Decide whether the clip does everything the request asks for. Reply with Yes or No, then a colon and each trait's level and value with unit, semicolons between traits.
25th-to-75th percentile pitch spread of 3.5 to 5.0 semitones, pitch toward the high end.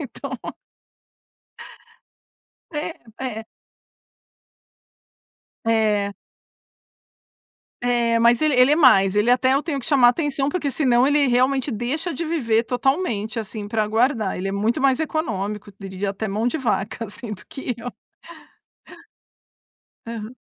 Yes: average, 4.2 semitones; high, 240 Hz